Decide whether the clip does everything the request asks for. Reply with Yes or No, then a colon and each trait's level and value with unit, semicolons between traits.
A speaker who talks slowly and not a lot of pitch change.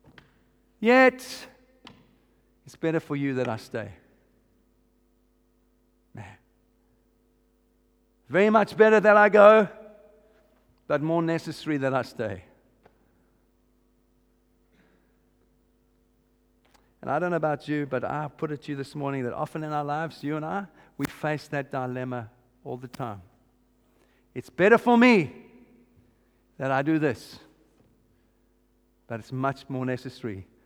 No: slow, 125 wpm; wide, 5.4 semitones